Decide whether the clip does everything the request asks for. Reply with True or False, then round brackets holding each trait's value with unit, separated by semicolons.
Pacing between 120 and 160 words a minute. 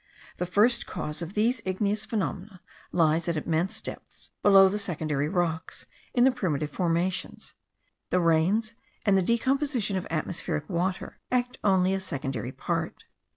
True (145 wpm)